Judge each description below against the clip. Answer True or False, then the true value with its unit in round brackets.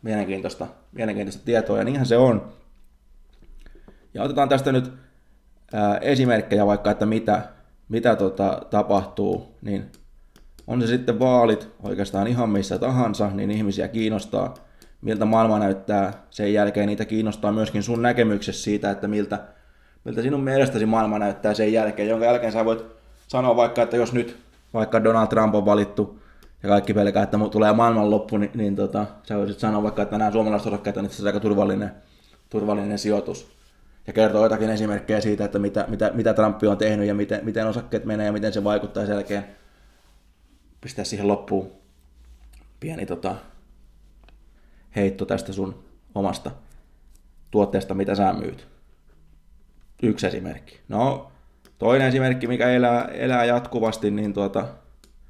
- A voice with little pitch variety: True (1.7 semitones)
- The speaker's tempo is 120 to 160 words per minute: True (150 wpm)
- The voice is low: True (105 Hz)